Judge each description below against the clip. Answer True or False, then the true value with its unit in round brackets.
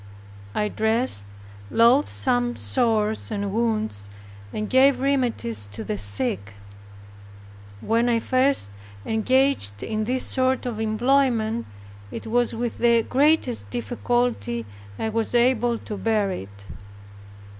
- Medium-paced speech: False (115 wpm)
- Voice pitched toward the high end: True (225 Hz)